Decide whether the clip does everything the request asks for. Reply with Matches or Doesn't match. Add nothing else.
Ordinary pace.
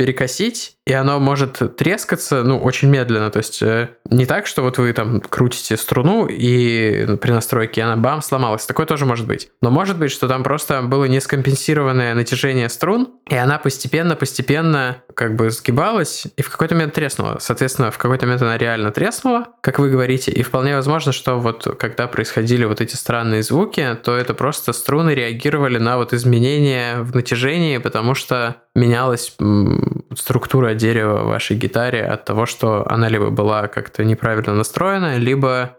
Doesn't match